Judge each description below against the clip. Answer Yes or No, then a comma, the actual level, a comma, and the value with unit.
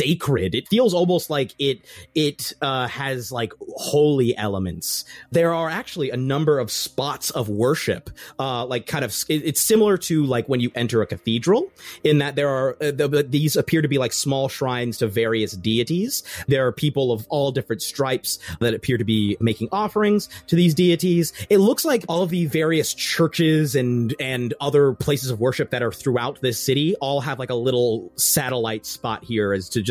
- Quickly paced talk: No, average, 195 wpm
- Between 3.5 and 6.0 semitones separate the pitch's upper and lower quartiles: Yes, average, 4.8 semitones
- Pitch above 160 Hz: No, low, 135 Hz